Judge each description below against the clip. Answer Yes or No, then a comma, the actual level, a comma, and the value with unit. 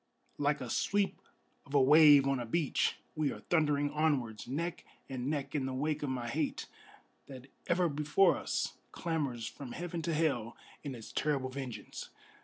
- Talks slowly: No, average, 170 wpm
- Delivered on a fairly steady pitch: No, average, 3.1 semitones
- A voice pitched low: No, medium, 145 Hz